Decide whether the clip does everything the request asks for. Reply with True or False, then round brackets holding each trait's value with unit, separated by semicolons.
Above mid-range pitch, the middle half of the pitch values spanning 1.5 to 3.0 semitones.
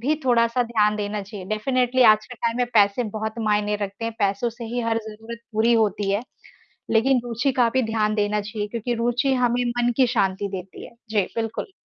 True (225 Hz; 2.5 semitones)